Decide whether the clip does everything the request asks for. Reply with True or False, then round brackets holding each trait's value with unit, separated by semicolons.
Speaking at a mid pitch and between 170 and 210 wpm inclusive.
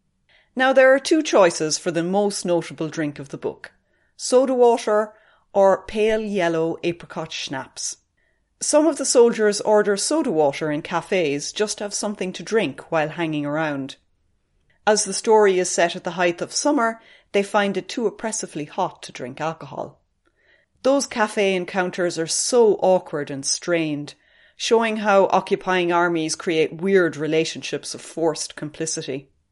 False (180 Hz; 150 wpm)